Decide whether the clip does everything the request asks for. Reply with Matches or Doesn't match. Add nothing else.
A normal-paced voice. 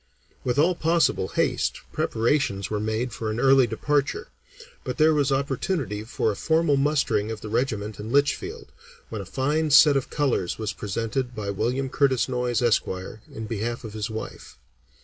Matches